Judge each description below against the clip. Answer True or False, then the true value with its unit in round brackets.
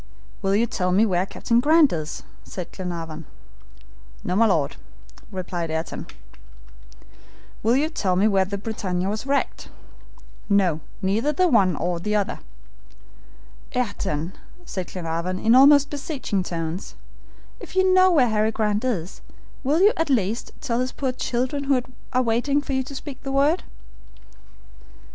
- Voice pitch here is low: False (215 Hz)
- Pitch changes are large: True (6.8 semitones)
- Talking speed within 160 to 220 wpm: False (150 wpm)